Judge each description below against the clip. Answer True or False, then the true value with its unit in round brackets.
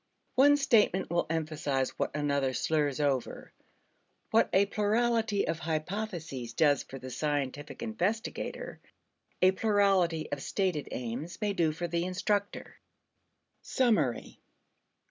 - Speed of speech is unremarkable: False (115 wpm)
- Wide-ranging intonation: True (6.0 semitones)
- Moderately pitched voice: True (170 Hz)